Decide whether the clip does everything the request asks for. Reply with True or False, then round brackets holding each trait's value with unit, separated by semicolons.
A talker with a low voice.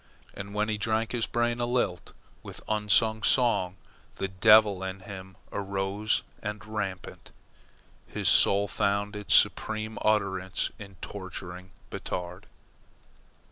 True (100 Hz)